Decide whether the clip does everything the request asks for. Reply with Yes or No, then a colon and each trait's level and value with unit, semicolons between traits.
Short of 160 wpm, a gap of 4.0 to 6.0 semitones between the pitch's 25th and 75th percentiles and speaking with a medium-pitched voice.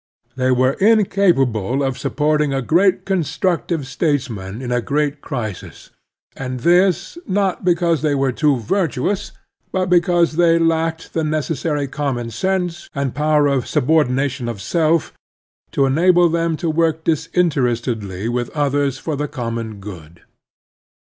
Yes: average, 145 wpm; average, 4.8 semitones; medium, 150 Hz